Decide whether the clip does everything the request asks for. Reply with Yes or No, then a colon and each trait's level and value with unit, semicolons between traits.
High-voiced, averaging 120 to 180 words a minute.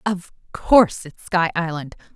No: medium, 175 Hz; average, 140 wpm